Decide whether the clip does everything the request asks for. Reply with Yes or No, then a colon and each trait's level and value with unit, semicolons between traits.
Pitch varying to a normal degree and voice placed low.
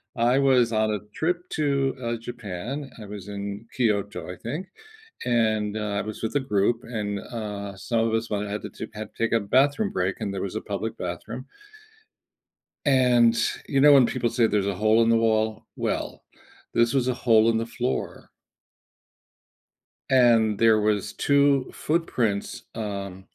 Yes: average, 3.3 semitones; low, 115 Hz